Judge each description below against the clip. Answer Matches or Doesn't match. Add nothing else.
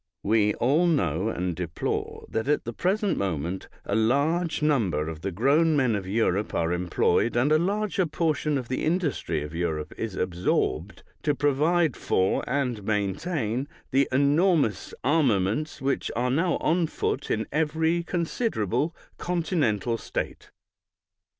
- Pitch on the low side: Matches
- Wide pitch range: Matches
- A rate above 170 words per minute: Doesn't match